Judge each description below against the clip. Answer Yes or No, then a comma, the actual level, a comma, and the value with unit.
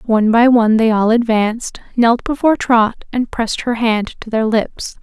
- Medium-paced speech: Yes, average, 190 wpm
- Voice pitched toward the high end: Yes, high, 230 Hz